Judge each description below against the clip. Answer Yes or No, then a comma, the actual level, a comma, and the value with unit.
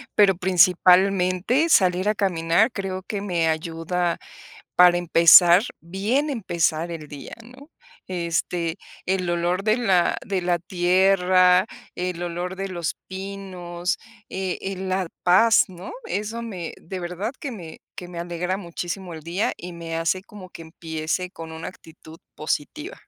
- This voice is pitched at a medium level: Yes, medium, 180 Hz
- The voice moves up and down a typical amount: No, narrow, 2.1 semitones